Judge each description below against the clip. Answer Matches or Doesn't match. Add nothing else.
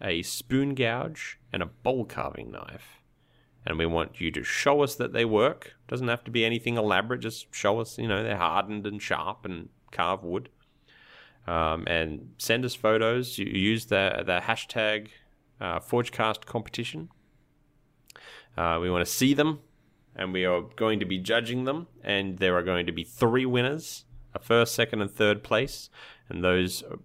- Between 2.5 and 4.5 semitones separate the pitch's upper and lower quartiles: Doesn't match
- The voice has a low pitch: Matches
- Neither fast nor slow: Matches